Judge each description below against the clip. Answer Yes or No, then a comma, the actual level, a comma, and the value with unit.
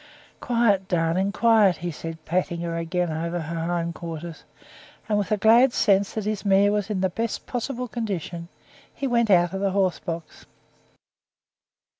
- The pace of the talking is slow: No, average, 165 wpm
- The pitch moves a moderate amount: Yes, average, 4.0 semitones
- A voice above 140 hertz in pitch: Yes, high, 190 Hz